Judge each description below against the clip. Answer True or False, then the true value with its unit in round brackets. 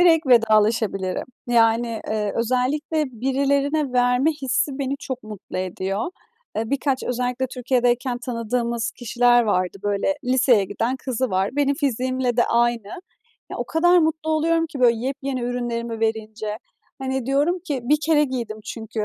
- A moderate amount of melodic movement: True (3.3 semitones)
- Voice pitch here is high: True (245 Hz)